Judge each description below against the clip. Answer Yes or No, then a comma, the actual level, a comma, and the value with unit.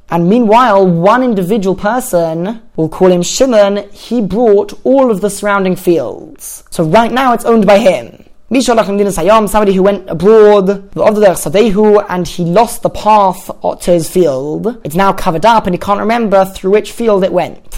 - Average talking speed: Yes, average, 170 wpm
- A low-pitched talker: No, high, 205 Hz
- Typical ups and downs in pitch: Yes, average, 3.2 semitones